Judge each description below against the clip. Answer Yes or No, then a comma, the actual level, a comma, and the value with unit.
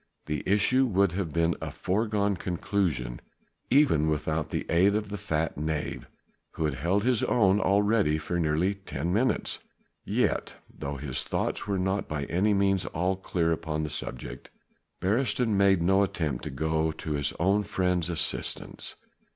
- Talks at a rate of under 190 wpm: Yes, average, 160 wpm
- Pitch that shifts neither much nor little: Yes, average, 4.5 semitones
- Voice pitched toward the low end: Yes, very low, 90 Hz